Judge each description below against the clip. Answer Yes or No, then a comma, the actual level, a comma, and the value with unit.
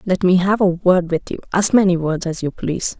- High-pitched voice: No, medium, 180 Hz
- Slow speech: No, fast, 240 wpm